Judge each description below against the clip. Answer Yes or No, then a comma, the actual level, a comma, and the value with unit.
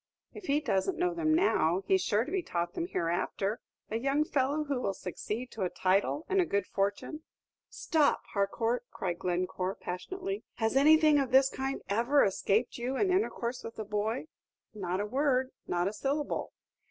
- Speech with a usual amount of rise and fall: No, wide, 7.2 semitones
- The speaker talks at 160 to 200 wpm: Yes, average, 180 wpm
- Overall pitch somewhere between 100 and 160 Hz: No, high, 240 Hz